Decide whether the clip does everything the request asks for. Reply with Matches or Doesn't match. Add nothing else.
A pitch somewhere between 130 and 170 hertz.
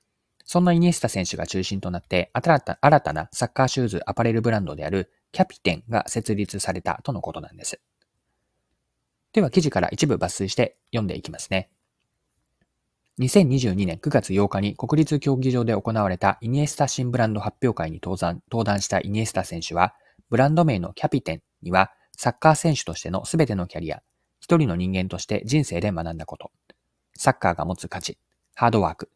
Doesn't match